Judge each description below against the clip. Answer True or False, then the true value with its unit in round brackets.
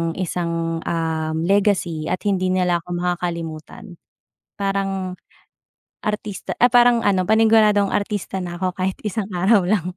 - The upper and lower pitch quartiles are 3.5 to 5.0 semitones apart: False (2.9 semitones)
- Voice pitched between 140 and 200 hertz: True (185 Hz)